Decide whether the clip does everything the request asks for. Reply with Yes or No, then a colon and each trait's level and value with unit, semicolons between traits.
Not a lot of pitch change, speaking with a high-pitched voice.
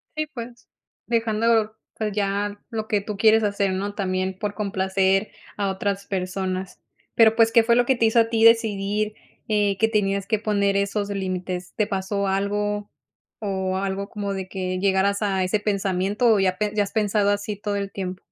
Yes: narrow, 1.9 semitones; high, 200 Hz